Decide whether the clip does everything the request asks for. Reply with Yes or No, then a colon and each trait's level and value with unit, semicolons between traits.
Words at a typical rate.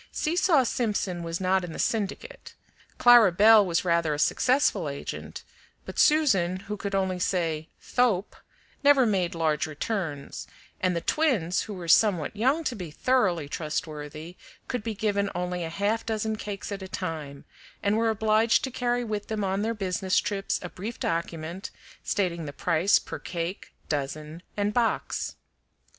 Yes: average, 160 wpm